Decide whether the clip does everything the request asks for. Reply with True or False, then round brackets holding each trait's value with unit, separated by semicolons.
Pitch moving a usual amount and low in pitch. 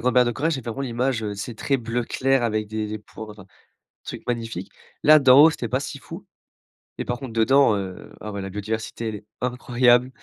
True (3.0 semitones; 120 Hz)